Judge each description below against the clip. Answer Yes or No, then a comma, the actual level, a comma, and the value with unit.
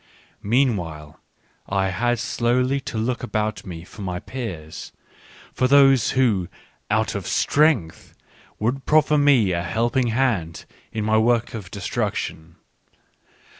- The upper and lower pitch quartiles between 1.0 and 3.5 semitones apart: No, wide, 5.5 semitones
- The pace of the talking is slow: Yes, slow, 130 wpm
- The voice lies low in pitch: Yes, low, 115 Hz